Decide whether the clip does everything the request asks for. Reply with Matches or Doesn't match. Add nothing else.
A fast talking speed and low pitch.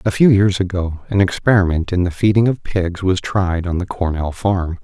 Matches